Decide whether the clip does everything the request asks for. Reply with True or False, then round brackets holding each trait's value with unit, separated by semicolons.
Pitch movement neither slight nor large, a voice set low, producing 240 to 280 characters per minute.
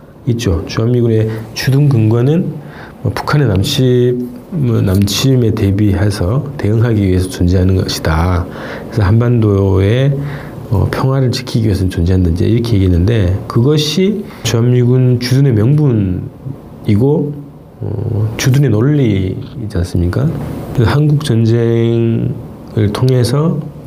True (5.0 semitones; 115 Hz; 255 characters per minute)